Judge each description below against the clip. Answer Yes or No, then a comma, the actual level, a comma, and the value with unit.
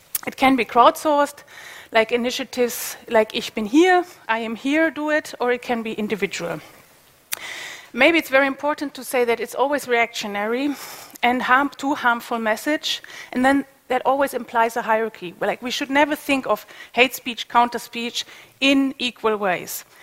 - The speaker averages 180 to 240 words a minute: No, average, 165 wpm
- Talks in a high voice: Yes, very high, 250 Hz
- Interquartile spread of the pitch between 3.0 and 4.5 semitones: Yes, average, 3.7 semitones